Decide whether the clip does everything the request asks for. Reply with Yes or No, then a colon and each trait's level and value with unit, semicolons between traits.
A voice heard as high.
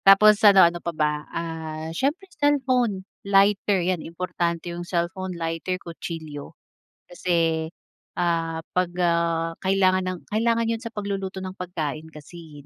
No: medium, 175 Hz